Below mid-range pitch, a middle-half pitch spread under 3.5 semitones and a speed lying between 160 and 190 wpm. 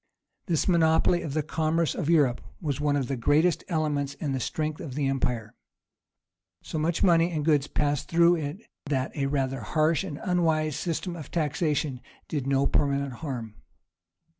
No: medium, 150 Hz; average, 2.9 semitones; average, 165 wpm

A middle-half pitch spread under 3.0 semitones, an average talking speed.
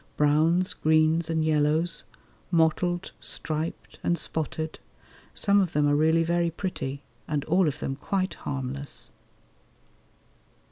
No: narrow, 2.4 semitones; slow, 120 wpm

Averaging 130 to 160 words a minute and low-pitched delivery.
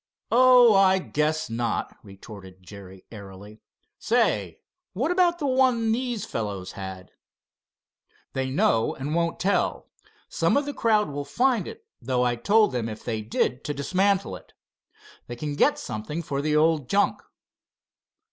No: average, 145 wpm; medium, 150 Hz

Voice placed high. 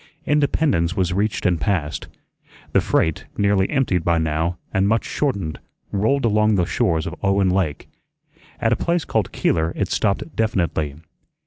No: very low, 95 Hz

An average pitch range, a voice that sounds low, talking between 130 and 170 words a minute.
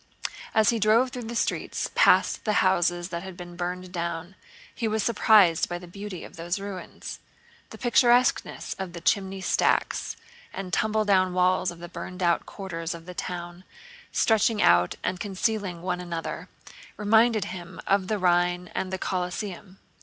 No: average, 3.0 semitones; medium, 185 Hz; average, 165 wpm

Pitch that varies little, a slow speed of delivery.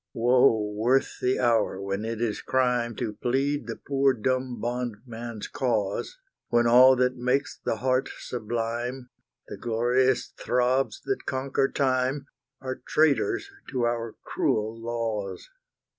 Yes: narrow, 2.3 semitones; slow, 130 wpm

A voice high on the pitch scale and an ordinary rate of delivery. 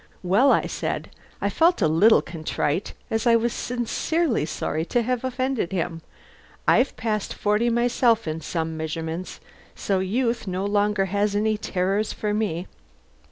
Yes: high, 210 Hz; average, 150 wpm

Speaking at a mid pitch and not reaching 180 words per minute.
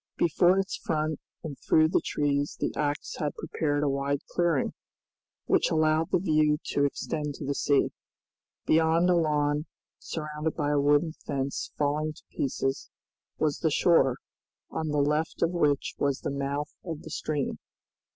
Yes: medium, 150 Hz; average, 160 wpm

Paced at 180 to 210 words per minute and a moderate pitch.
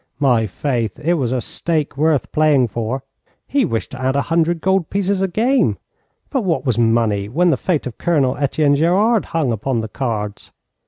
Yes: average, 190 wpm; medium, 145 Hz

